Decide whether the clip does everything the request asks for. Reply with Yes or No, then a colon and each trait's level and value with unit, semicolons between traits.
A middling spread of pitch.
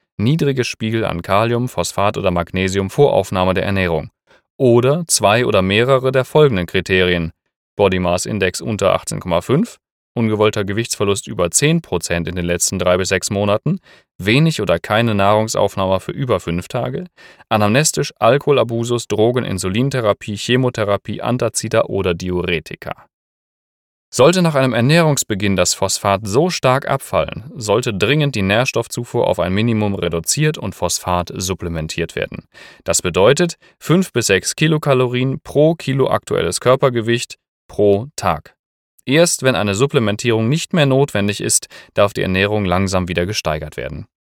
No: wide, 6.0 semitones